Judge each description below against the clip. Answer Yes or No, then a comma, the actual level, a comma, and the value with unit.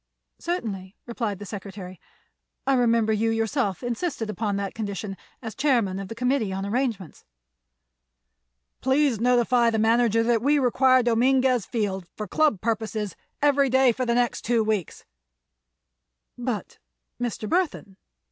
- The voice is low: No, high, 230 Hz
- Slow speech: Yes, slow, 130 wpm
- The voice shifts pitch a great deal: No, average, 3.6 semitones